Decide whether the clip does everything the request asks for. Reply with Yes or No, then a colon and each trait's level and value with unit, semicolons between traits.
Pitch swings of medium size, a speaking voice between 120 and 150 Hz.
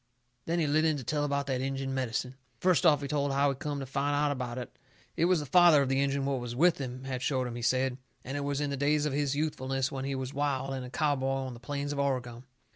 No: narrow, 1.8 semitones; medium, 140 Hz